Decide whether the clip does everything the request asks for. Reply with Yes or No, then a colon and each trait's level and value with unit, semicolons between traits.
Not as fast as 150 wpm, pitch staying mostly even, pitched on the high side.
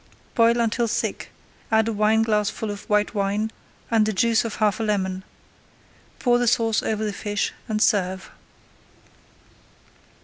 Yes: average, 140 wpm; narrow, 1.7 semitones; high, 215 Hz